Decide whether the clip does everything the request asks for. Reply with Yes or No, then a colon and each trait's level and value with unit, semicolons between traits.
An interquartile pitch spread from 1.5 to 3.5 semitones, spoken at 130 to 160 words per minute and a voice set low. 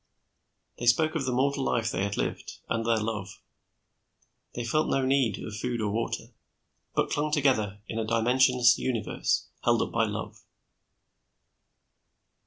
Yes: average, 3.0 semitones; average, 150 wpm; low, 120 Hz